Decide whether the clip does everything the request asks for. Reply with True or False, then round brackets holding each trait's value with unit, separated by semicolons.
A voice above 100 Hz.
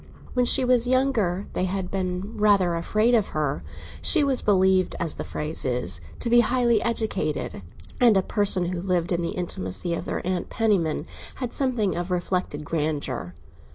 True (185 Hz)